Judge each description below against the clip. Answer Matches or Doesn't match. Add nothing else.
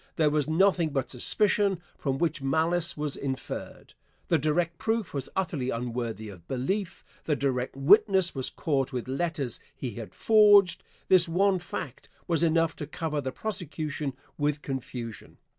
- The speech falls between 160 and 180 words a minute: Doesn't match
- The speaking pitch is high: Doesn't match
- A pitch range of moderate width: Matches